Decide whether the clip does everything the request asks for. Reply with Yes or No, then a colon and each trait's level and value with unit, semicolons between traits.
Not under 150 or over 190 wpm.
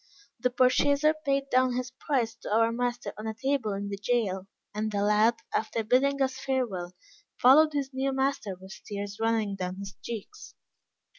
Yes: average, 170 wpm